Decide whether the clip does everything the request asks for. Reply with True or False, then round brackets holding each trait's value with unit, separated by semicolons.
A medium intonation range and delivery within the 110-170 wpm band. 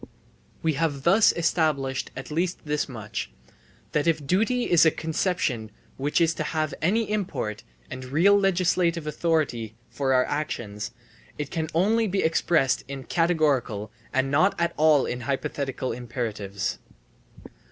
True (4.4 semitones; 140 wpm)